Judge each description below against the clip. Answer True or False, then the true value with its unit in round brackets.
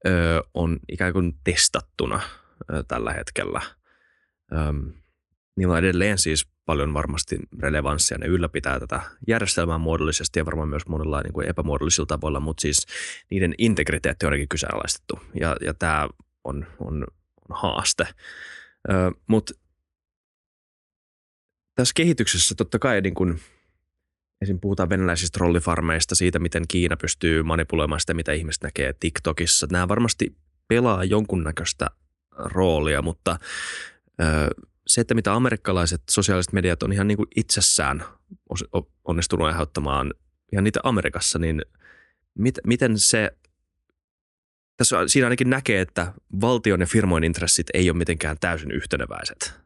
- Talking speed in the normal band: True (120 wpm)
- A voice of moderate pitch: False (85 Hz)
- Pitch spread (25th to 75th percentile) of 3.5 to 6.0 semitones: True (4.0 semitones)